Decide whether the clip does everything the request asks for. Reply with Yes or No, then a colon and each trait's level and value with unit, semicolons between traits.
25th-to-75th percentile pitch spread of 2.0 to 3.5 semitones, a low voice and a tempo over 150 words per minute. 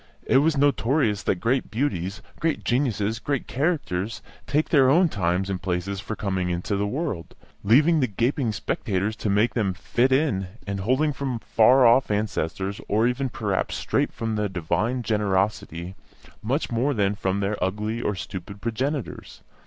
No: average, 5.0 semitones; low, 110 Hz; average, 160 wpm